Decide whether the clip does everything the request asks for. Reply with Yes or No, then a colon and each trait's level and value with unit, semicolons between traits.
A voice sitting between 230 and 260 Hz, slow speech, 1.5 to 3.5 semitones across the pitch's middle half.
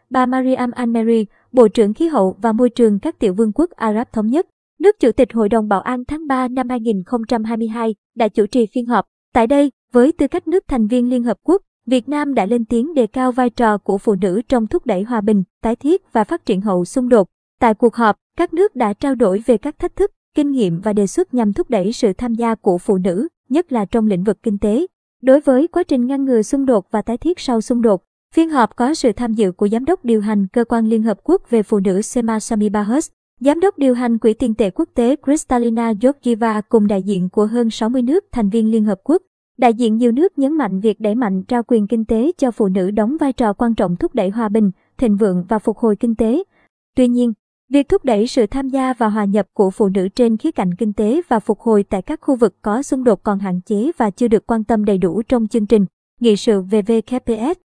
No: high, 235 Hz; average, 245 wpm; average, 3.2 semitones